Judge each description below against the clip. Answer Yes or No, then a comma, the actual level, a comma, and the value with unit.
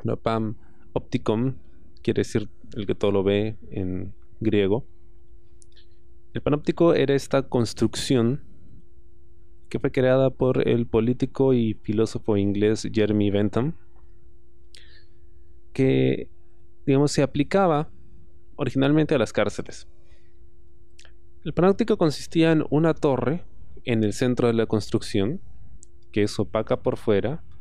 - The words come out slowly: Yes, slow, 115 wpm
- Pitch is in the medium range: No, low, 110 Hz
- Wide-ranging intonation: Yes, wide, 7.2 semitones